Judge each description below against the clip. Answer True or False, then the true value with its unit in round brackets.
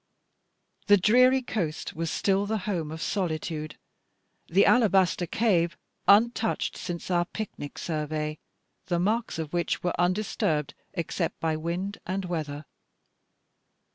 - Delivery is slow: True (125 wpm)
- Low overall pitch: False (175 Hz)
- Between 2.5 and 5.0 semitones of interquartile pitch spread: True (4.2 semitones)